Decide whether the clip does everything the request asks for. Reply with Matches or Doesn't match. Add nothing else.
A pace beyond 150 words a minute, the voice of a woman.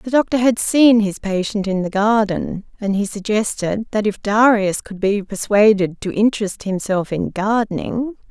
Matches